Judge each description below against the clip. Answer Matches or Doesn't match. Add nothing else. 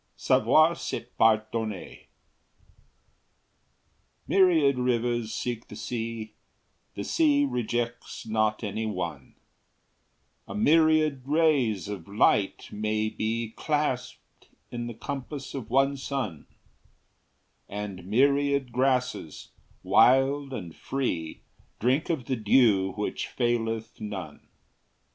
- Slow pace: Matches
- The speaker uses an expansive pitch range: Doesn't match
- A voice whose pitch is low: Matches